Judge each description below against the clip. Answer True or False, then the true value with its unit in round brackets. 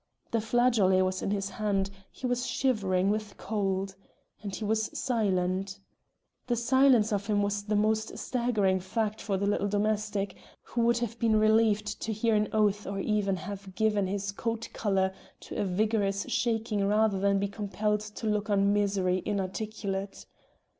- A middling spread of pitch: False (1.9 semitones)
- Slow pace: False (165 wpm)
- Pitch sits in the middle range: False (205 Hz)